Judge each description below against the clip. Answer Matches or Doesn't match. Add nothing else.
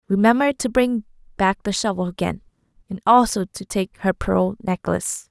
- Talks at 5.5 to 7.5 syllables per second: Doesn't match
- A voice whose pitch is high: Matches